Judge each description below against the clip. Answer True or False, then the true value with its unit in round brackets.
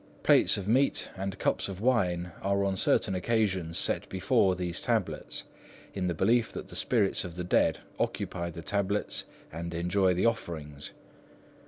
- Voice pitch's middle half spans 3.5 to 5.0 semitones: False (2.6 semitones)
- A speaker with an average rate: True (160 wpm)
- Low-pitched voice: True (95 Hz)